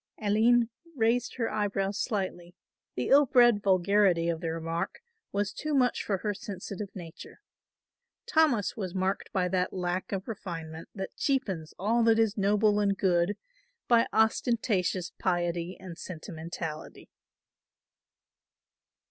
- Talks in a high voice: Yes, high, 195 Hz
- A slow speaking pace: Yes, slow, 125 wpm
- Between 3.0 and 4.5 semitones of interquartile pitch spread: Yes, average, 4.0 semitones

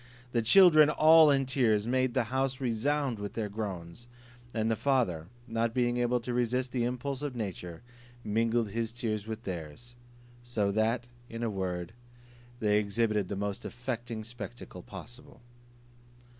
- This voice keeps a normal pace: Yes, average, 150 wpm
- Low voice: Yes, low, 115 Hz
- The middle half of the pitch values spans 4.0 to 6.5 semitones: No, average, 3.2 semitones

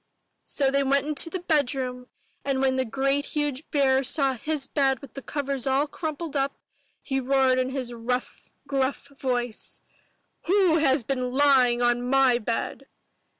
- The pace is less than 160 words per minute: No, average, 165 wpm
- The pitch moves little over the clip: Yes, narrow, 1.9 semitones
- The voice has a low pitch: No, very high, 270 Hz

